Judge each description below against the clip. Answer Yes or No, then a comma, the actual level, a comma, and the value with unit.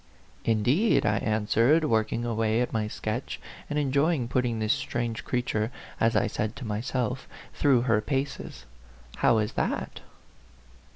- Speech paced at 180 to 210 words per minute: No, average, 155 wpm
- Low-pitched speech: Yes, low, 115 Hz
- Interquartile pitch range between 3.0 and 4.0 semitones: Yes, average, 3.3 semitones